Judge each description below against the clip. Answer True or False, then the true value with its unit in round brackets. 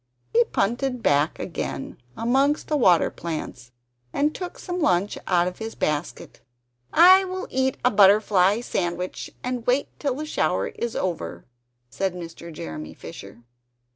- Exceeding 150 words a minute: False (140 wpm)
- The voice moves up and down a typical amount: False (7.4 semitones)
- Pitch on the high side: True (205 Hz)